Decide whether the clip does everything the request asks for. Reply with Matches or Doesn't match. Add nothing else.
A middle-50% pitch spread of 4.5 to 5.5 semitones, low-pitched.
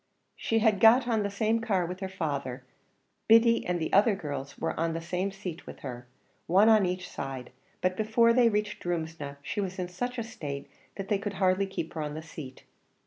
Doesn't match